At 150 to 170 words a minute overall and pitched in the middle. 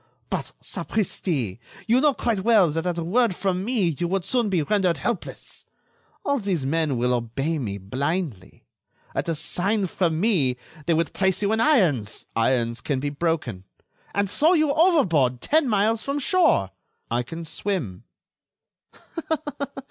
Yes: average, 155 wpm; medium, 175 Hz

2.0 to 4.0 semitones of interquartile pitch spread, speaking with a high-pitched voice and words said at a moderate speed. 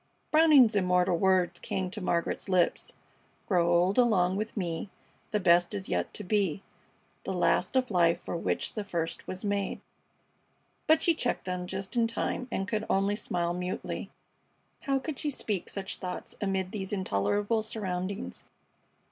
Yes: average, 3.1 semitones; high, 195 Hz; average, 155 wpm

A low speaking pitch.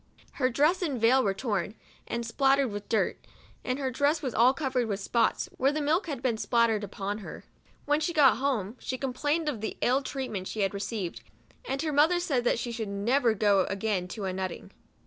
No: high, 245 Hz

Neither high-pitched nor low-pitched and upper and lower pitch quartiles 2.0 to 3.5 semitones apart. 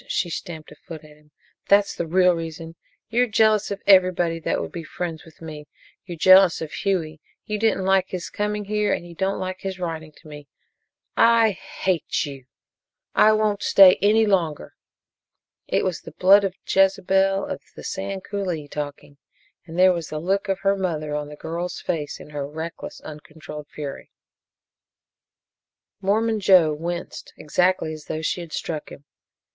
No: medium, 175 Hz; average, 3.9 semitones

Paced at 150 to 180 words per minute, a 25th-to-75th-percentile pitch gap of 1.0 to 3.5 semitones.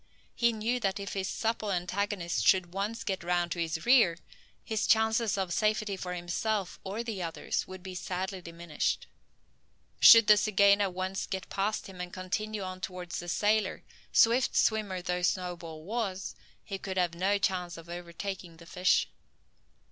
Yes: average, 165 wpm; average, 2.9 semitones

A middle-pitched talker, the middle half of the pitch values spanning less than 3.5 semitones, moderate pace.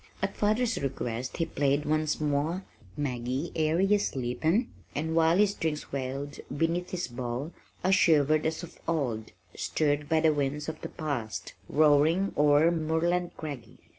Yes: medium, 155 Hz; average, 2.9 semitones; average, 150 wpm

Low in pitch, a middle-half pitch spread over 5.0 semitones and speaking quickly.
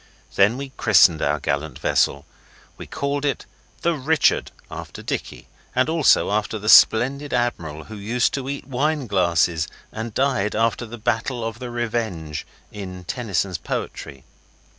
No: low, 115 Hz; wide, 5.4 semitones; average, 145 wpm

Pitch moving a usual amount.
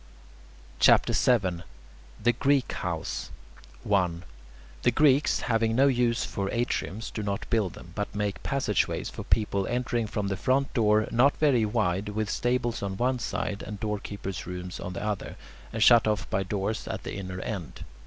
Yes: average, 3.5 semitones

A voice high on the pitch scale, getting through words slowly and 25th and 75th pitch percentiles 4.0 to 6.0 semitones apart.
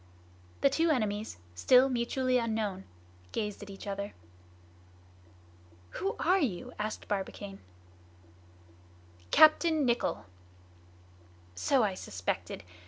Yes: high, 225 Hz; slow, 95 wpm; average, 4.8 semitones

